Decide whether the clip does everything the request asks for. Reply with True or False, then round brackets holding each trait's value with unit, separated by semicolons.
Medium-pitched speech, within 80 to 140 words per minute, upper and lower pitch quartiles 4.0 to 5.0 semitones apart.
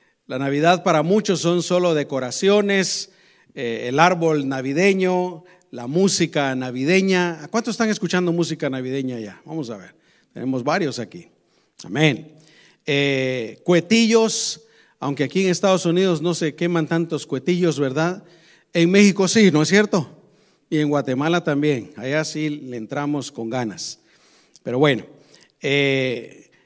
True (160 Hz; 135 wpm; 4.7 semitones)